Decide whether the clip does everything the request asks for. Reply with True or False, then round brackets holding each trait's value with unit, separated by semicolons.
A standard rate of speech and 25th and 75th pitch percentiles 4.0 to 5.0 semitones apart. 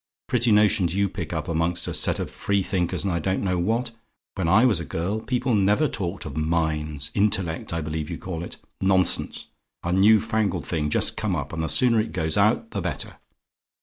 False (210 wpm; 4.4 semitones)